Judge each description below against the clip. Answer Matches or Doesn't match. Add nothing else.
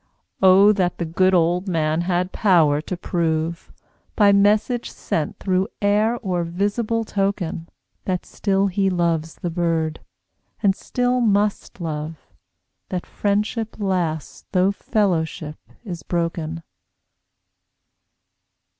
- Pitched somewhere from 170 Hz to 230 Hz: Matches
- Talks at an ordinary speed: Doesn't match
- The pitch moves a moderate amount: Matches